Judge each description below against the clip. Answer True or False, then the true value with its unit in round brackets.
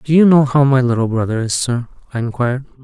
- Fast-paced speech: True (235 wpm)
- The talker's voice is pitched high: False (130 Hz)